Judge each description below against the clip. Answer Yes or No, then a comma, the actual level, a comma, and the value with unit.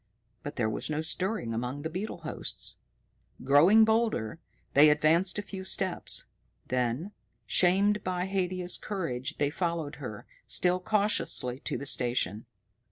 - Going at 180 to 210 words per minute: No, slow, 135 wpm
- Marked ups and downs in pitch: Yes, wide, 5.8 semitones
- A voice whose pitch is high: No, medium, 165 Hz